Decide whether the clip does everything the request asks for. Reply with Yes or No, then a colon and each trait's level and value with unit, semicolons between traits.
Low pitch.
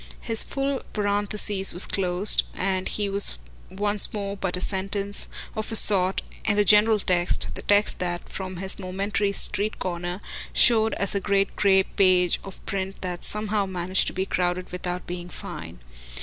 No: high, 195 Hz